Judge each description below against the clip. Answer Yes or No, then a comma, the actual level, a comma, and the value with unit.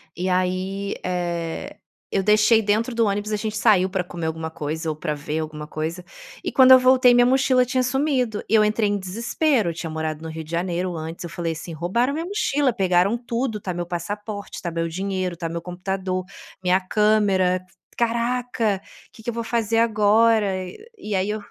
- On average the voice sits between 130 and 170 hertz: No, high, 195 Hz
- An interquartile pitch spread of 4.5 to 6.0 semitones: Yes, average, 4.9 semitones